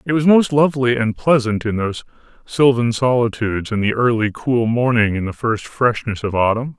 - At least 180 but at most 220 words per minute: Yes, average, 185 wpm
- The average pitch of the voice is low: Yes, low, 120 Hz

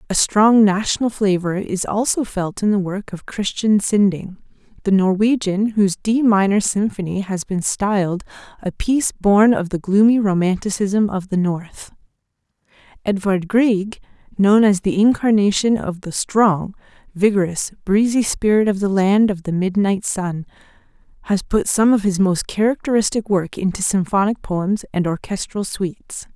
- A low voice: No, high, 200 Hz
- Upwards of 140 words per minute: Yes, average, 150 wpm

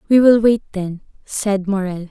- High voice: Yes, high, 200 Hz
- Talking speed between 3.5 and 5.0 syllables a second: Yes, 4.5 syllables/s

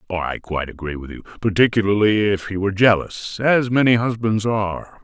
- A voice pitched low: Yes, low, 105 Hz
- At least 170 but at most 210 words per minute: No, average, 155 wpm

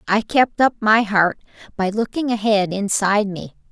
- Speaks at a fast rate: No, average, 160 wpm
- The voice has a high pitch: Yes, high, 210 Hz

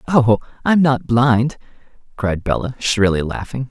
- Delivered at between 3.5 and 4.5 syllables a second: Yes, 4.1 syllables/s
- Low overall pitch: Yes, low, 120 Hz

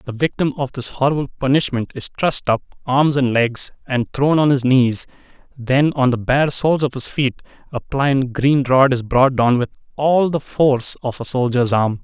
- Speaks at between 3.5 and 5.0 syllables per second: Yes, 4.7 syllables/s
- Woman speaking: No, male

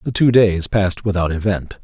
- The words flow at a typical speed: Yes, average, 195 wpm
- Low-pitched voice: Yes, low, 100 Hz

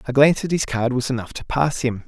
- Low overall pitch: Yes, low, 130 Hz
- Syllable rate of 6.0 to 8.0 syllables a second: Yes, 6.3 syllables/s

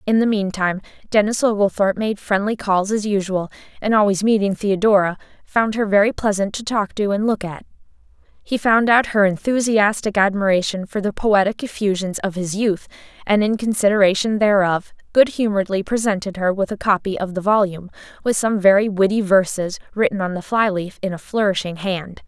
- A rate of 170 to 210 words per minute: Yes, average, 175 wpm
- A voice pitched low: No, high, 200 Hz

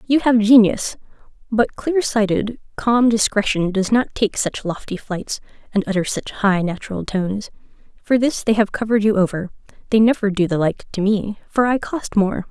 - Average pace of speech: Yes, average, 175 wpm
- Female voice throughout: Yes, female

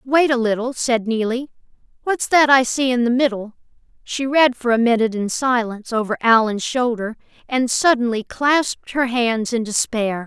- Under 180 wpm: Yes, average, 170 wpm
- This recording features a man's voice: No, female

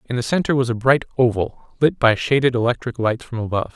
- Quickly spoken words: Yes, fast, 225 wpm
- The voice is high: No, low, 125 Hz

